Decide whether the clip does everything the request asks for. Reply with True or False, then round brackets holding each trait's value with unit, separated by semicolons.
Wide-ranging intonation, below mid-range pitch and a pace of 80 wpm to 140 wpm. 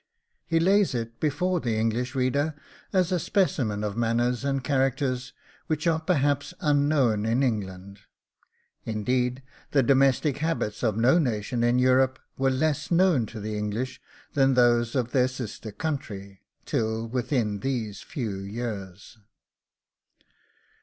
False (4.2 semitones; 125 Hz; 135 wpm)